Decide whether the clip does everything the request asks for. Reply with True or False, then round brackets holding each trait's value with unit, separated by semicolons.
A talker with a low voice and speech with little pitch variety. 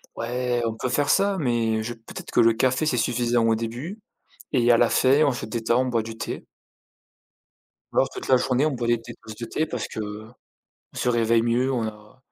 True (120 Hz; 2.1 semitones)